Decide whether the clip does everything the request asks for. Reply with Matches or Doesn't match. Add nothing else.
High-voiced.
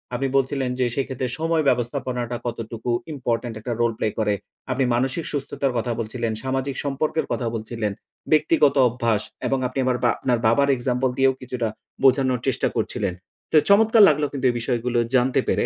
Doesn't match